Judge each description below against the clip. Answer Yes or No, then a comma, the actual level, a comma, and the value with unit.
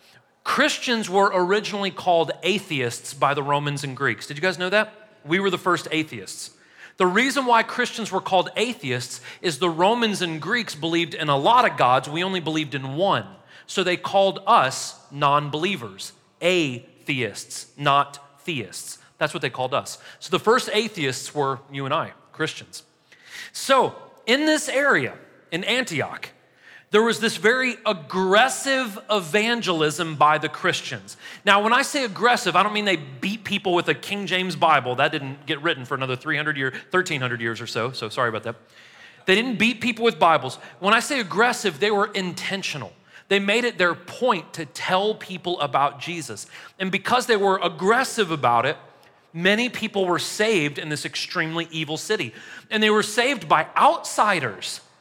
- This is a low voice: No, medium, 180 Hz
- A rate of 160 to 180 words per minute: Yes, average, 170 wpm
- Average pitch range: No, wide, 6.5 semitones